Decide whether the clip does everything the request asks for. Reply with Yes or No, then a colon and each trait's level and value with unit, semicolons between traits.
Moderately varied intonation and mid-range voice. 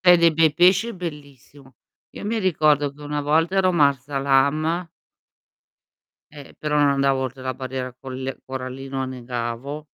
Yes: average, 3.2 semitones; medium, 145 Hz